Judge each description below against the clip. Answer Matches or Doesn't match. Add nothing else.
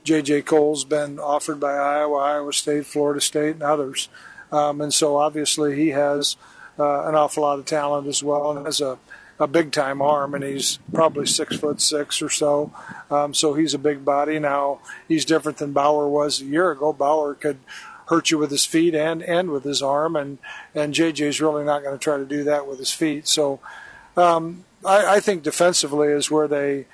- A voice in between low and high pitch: Matches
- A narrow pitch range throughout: Matches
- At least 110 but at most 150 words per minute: Doesn't match